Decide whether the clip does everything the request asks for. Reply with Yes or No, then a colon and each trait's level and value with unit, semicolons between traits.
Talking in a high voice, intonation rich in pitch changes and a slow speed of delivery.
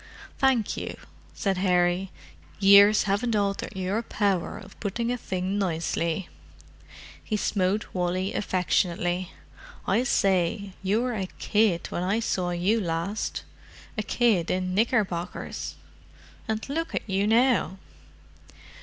No: high, 195 Hz; average, 3.0 semitones; slow, 120 wpm